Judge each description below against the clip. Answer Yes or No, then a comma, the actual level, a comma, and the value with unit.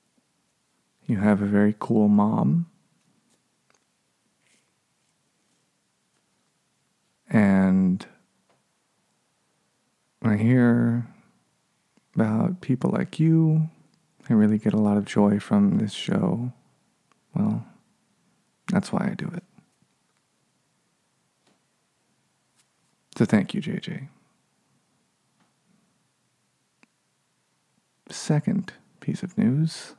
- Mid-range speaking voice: Yes, medium, 160 Hz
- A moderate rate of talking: No, slow, 75 wpm